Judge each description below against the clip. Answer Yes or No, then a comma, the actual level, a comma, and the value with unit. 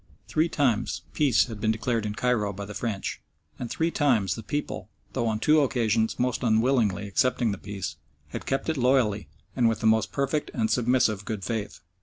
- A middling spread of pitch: Yes, average, 3.4 semitones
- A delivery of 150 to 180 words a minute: No, average, 190 wpm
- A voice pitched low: Yes, low, 115 Hz